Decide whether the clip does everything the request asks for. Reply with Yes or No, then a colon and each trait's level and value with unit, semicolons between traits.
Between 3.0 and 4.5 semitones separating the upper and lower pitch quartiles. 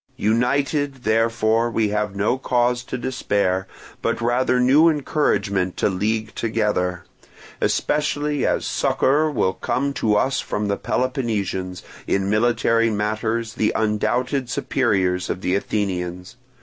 Yes: average, 3.9 semitones